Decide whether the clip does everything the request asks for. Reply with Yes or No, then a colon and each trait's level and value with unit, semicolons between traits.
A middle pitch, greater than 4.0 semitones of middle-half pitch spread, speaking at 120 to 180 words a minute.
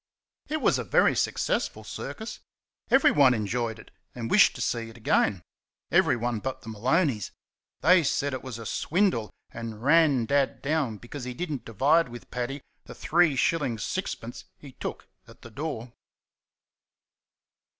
No: low, 130 Hz; average, 5.0 semitones; average, 150 wpm